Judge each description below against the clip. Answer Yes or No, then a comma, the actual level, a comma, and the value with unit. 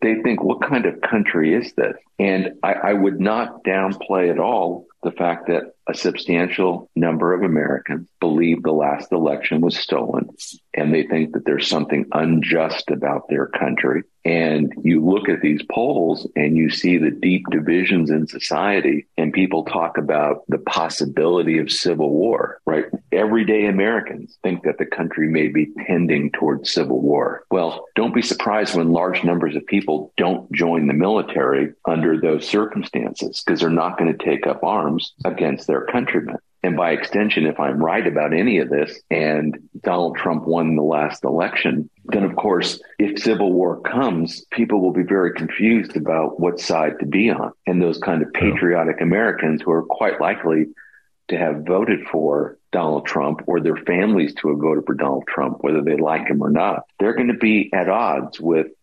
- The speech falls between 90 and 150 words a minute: No, average, 180 wpm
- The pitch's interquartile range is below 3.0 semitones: No, average, 3.4 semitones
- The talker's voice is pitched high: No, very low, 85 Hz